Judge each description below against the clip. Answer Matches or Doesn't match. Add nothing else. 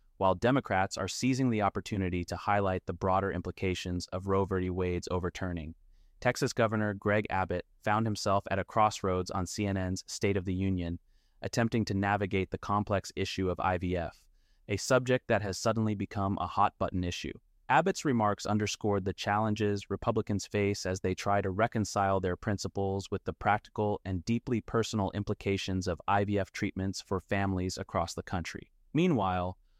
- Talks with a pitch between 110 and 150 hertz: Doesn't match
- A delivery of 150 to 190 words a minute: Matches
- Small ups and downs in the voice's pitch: Matches